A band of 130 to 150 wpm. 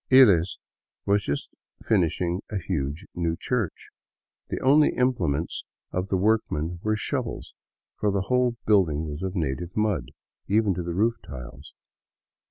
Yes: average, 140 wpm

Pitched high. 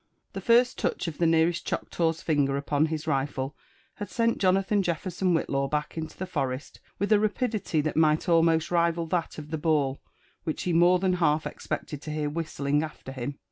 No: medium, 160 Hz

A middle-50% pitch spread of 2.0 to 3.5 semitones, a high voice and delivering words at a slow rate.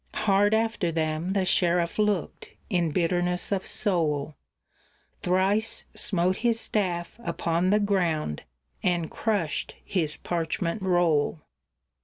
No: average, 3.2 semitones; medium, 180 Hz; slow, 110 wpm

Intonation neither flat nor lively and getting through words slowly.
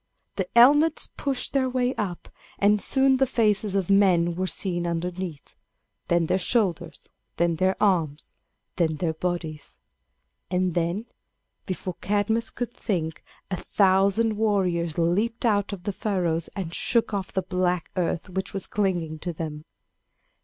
No: average, 3.4 semitones; average, 145 wpm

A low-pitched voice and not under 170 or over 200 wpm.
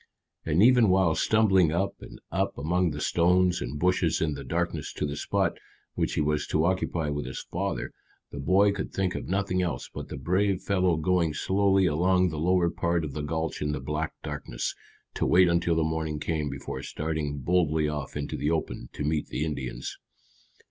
Yes: very low, 80 Hz; average, 195 wpm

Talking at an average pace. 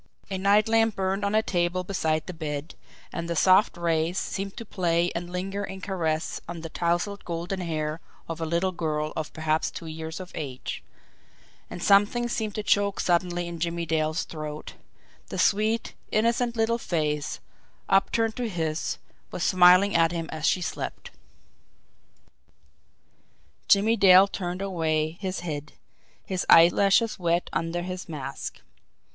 Yes: average, 150 wpm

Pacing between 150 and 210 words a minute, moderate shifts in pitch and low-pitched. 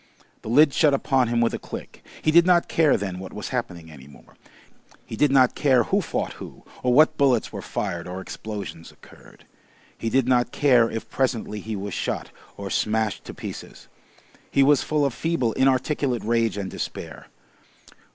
Yes: average, 180 wpm; average, 4.7 semitones; low, 120 Hz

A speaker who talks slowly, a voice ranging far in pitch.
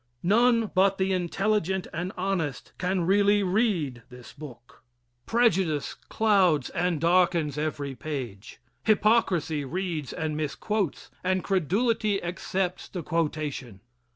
No: slow, 110 wpm; average, 4.5 semitones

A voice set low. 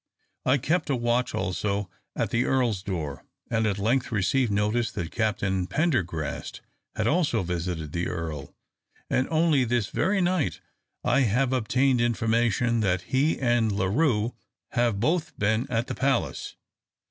Yes: low, 115 Hz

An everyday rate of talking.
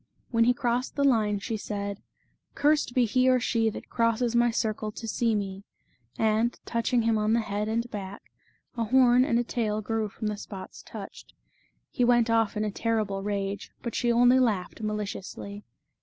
Yes: average, 185 wpm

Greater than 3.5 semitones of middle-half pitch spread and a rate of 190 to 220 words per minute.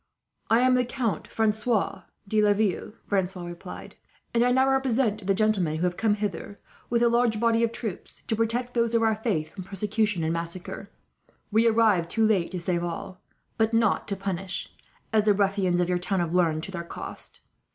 Yes: average, 3.9 semitones; average, 195 wpm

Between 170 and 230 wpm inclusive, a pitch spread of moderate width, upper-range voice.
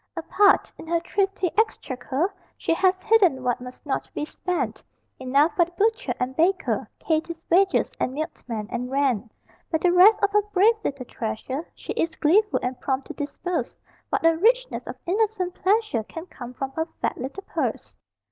No: average, 175 wpm; wide, 6.6 semitones; very high, 330 Hz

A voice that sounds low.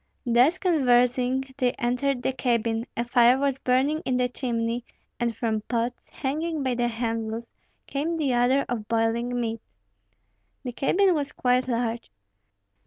No: high, 245 Hz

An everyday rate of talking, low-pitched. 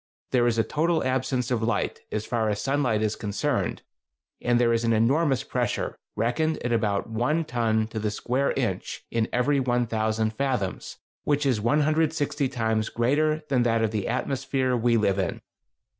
Yes: average, 170 wpm; low, 120 Hz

